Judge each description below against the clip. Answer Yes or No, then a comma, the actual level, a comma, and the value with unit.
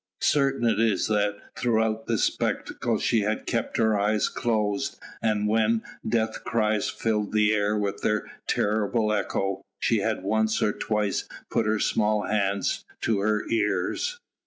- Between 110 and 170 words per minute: Yes, average, 150 wpm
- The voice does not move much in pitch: Yes, narrow, 1.3 semitones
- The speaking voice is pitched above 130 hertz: No, low, 110 Hz